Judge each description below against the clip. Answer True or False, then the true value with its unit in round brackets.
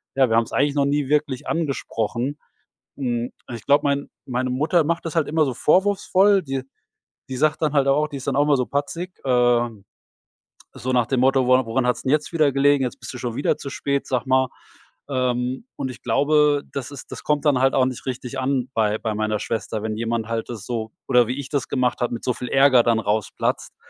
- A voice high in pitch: False (130 Hz)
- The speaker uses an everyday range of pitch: True (3.0 semitones)